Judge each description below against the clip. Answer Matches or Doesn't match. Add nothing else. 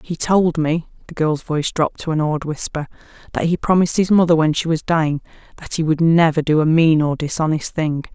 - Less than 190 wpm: Doesn't match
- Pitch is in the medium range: Matches